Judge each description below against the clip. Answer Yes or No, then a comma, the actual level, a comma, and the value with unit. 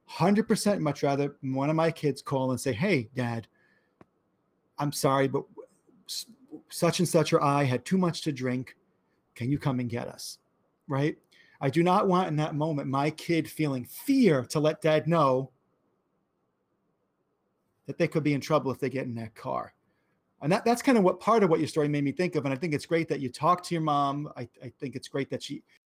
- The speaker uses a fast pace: Yes, fast, 215 wpm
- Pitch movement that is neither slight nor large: Yes, average, 3.8 semitones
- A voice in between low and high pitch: Yes, medium, 150 Hz